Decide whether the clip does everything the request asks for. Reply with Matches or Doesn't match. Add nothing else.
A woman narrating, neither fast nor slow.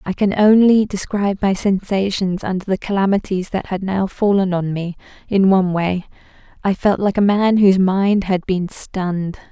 Matches